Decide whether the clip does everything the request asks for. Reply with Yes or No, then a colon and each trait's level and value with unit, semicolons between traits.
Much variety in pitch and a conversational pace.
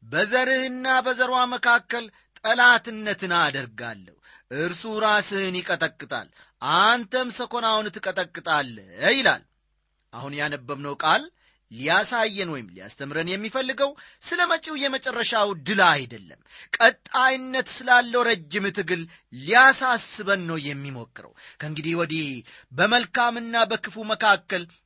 Yes: wide, 7.5 semitones; average, 85 wpm